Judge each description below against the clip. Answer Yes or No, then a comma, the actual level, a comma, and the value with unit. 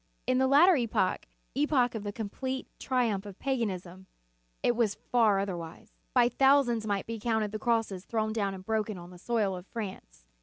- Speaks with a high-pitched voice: Yes, high, 220 Hz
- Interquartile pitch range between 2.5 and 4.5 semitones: Yes, average, 3.8 semitones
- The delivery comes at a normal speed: Yes, average, 180 wpm